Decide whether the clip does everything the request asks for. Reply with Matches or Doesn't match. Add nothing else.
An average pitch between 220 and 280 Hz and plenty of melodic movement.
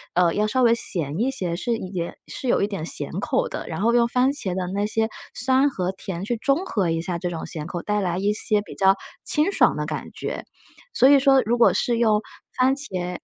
Doesn't match